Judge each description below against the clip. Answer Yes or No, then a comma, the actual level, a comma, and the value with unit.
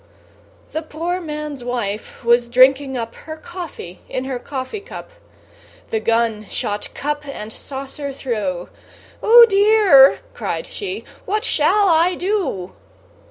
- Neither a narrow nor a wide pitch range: No, wide, 7.0 semitones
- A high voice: Yes, very high, 275 Hz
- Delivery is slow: Yes, slow, 125 wpm